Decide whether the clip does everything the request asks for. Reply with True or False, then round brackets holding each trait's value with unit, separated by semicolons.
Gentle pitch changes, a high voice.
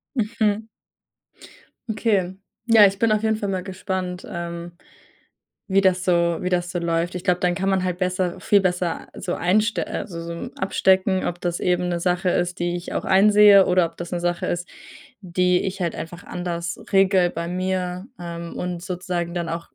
False (1.7 semitones; 180 Hz)